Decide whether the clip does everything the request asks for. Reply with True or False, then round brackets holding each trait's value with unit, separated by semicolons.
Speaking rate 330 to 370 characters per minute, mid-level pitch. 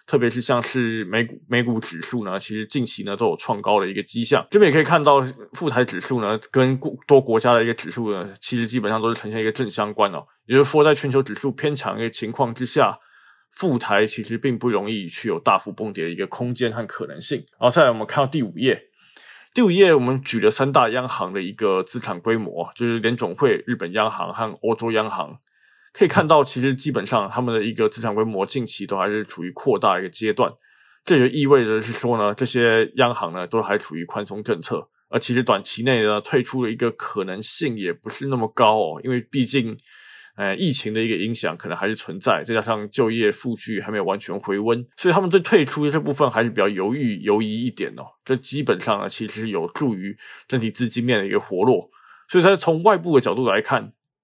False (335 characters per minute; 115 Hz)